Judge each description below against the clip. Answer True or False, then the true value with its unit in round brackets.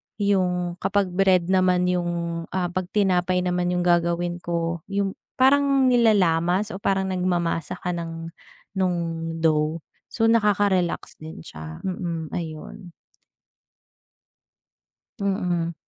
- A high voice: False (180 Hz)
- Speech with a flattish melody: True (2.2 semitones)